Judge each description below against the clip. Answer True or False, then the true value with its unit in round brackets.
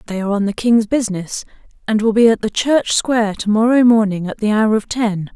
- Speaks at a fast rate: True (235 wpm)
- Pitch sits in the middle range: False (215 Hz)